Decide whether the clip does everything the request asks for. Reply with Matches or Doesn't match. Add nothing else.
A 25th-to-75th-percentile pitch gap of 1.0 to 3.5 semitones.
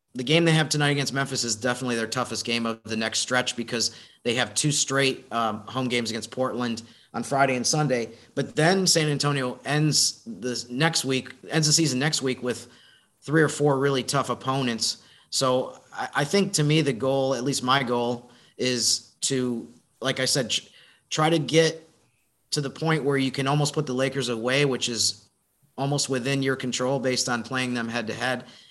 Matches